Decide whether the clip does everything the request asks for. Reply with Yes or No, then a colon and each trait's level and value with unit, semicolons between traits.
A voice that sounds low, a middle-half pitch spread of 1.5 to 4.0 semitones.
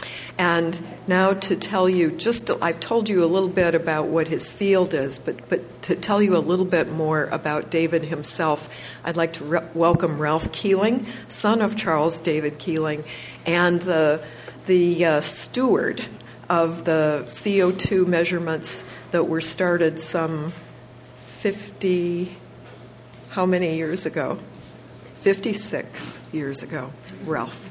No: medium, 165 Hz; average, 3.0 semitones